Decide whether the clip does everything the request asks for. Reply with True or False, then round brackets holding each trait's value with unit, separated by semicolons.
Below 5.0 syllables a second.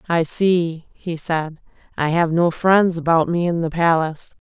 True (4.2 syllables/s)